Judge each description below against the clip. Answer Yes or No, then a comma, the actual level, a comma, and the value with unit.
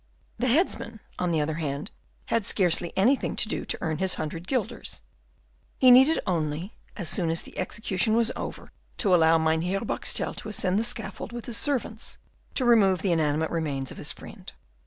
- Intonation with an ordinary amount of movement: No, wide, 6.0 semitones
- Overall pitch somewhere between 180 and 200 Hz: Yes, high, 190 Hz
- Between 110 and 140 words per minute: No, average, 180 wpm